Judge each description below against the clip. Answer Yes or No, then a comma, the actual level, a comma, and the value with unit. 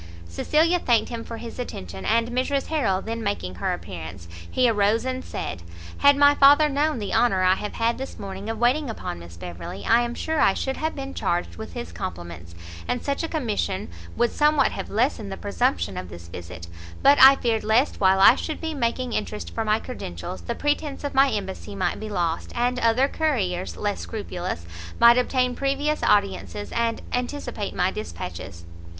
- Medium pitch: No, high, 225 Hz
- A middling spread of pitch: No, wide, 6.9 semitones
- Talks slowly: No, average, 190 wpm